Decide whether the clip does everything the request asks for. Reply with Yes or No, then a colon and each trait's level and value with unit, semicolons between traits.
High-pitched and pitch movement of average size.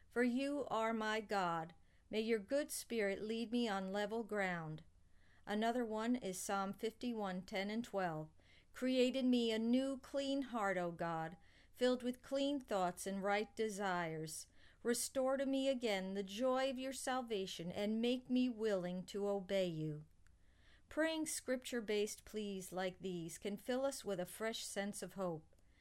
Yes: high, 210 Hz; average, 5.0 semitones